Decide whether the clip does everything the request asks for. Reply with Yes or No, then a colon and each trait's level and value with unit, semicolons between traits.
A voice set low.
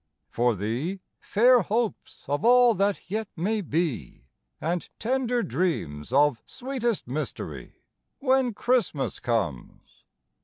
No: high, 190 Hz